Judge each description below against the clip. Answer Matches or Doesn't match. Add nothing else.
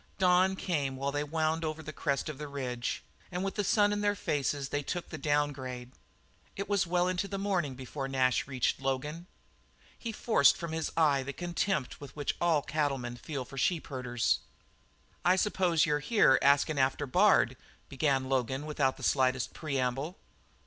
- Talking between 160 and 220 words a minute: Matches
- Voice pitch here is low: Doesn't match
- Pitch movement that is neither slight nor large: Matches